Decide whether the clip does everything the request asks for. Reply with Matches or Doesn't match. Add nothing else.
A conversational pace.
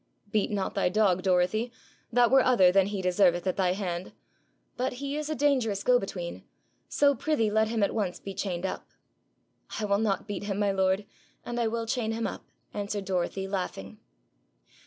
Matches